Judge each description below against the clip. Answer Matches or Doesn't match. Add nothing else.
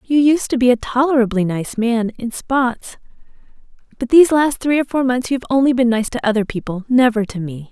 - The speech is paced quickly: Matches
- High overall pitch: Matches